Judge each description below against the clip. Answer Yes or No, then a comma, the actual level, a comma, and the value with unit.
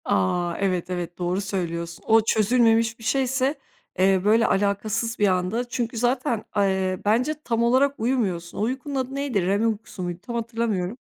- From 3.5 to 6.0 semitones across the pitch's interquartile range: Yes, average, 4.4 semitones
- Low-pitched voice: No, high, 220 Hz